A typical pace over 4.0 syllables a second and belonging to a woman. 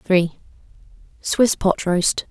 No: 3.0 syllables/s; female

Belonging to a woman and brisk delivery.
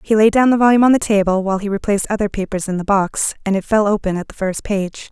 Yes: female; fast, 280 wpm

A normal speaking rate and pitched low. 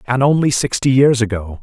Yes: average, 185 wpm; low, 125 Hz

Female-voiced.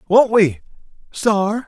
No: male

